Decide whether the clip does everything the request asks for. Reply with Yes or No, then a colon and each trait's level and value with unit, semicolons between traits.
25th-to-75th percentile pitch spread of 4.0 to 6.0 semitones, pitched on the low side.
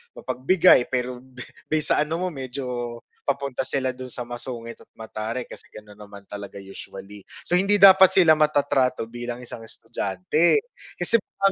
Yes: average, 4.7 semitones; low, 125 Hz